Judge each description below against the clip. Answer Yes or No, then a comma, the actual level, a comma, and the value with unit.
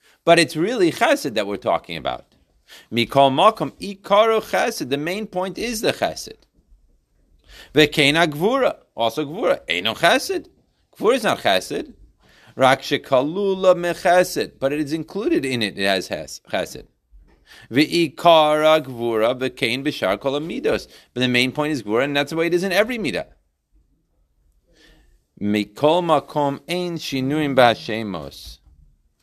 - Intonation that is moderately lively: No, wide, 7.3 semitones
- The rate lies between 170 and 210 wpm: No, average, 140 wpm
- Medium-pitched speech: Yes, medium, 150 Hz